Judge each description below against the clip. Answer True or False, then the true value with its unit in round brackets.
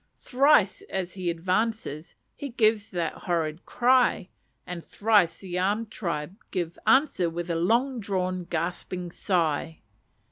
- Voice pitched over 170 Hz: True (185 Hz)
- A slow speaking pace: True (130 wpm)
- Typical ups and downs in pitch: True (4.4 semitones)